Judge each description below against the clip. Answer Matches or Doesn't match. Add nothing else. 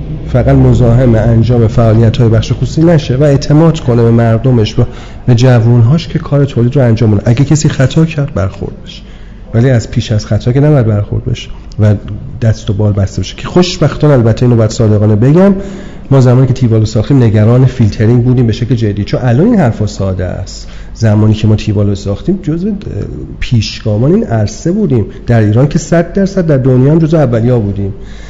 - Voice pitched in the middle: Doesn't match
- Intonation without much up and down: Doesn't match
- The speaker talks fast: Matches